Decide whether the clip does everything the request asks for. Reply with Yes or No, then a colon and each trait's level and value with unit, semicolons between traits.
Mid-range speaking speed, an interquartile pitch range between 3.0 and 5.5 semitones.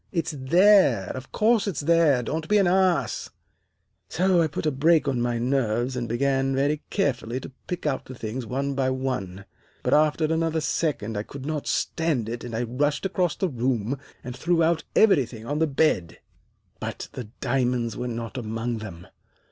Yes: average, 180 wpm; average, 5.1 semitones